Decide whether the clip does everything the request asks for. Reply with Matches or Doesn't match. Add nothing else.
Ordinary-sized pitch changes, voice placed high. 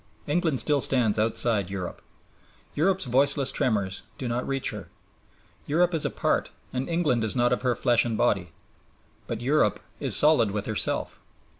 Doesn't match